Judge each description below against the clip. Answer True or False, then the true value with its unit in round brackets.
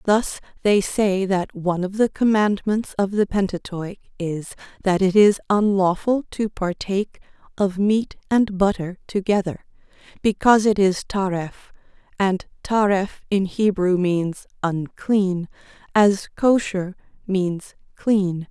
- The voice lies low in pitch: False (195 Hz)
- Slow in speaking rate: True (120 wpm)